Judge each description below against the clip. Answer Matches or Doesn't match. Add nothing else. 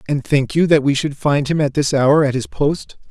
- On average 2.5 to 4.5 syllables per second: Doesn't match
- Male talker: Matches